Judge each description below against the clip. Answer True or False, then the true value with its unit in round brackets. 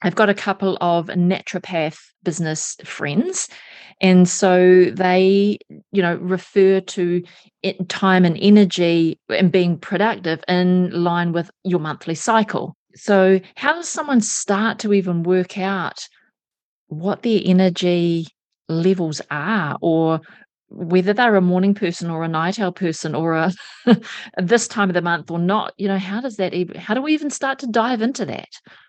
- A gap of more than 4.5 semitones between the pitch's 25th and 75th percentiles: False (2.9 semitones)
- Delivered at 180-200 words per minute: False (160 wpm)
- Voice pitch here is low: False (185 Hz)